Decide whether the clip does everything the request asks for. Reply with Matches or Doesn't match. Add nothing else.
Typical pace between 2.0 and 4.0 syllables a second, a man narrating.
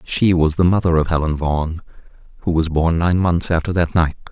Doesn't match